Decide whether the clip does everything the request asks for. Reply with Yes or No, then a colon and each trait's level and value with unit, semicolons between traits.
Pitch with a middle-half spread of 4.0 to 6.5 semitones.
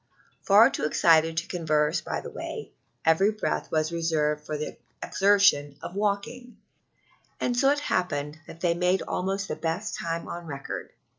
Yes: average, 4.3 semitones